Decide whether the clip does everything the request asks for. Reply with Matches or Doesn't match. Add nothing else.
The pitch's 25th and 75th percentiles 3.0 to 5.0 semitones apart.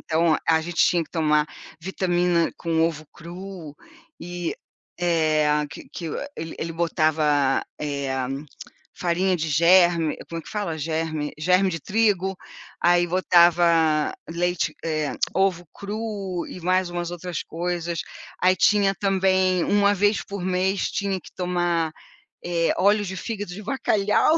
Doesn't match